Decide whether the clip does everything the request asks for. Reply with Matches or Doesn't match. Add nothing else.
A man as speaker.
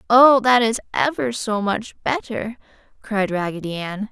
Doesn't match